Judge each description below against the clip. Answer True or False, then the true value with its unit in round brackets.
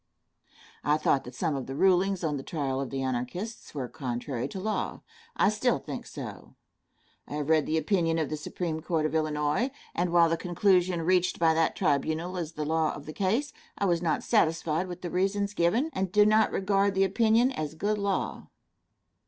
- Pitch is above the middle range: False (165 Hz)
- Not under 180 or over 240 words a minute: True (195 wpm)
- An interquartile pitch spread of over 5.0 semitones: False (4.1 semitones)